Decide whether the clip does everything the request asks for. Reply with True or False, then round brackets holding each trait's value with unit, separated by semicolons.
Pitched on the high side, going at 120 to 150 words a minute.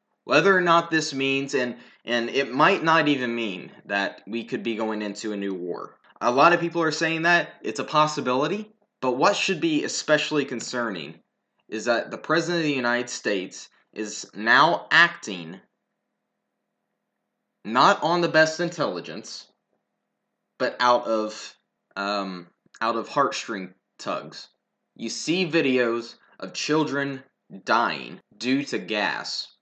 False (135 Hz; 140 wpm)